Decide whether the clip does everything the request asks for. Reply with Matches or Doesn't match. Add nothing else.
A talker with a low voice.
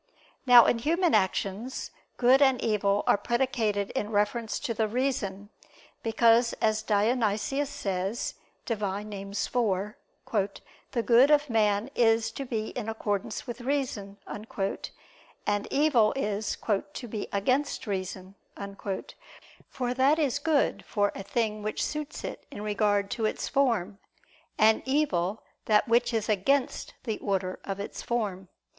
Doesn't match